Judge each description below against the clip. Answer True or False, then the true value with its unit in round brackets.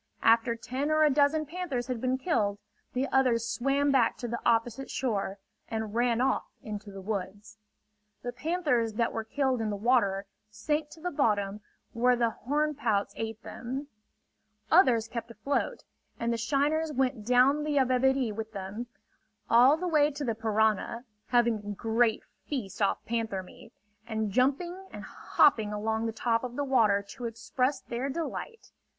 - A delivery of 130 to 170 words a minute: True (165 wpm)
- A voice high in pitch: True (240 Hz)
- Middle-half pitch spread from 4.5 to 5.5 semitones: False (3.8 semitones)